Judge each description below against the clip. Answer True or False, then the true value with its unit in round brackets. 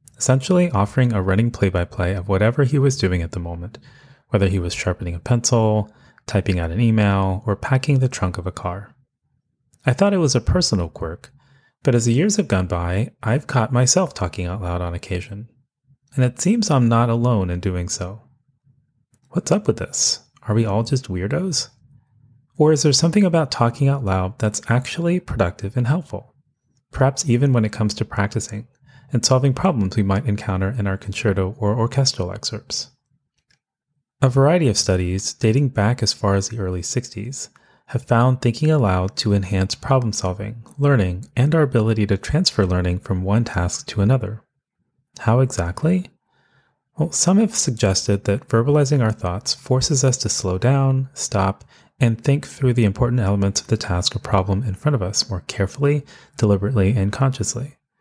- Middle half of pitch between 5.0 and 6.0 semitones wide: True (5.4 semitones)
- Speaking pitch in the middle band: False (115 Hz)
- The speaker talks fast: False (180 wpm)